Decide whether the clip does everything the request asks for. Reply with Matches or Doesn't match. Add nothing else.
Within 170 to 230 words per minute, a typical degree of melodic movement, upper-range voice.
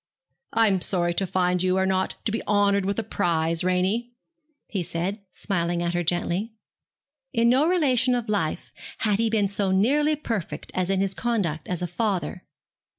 Matches